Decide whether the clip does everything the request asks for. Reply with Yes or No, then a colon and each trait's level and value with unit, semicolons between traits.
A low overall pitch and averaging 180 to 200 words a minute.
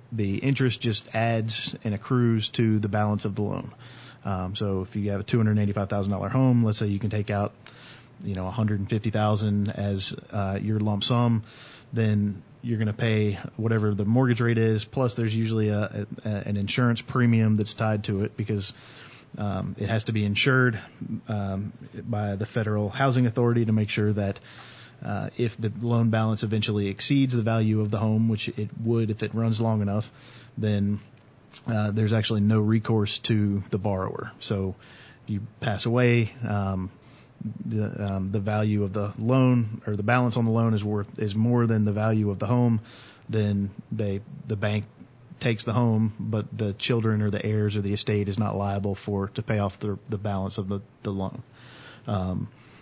Yes: low, 110 Hz; average, 195 wpm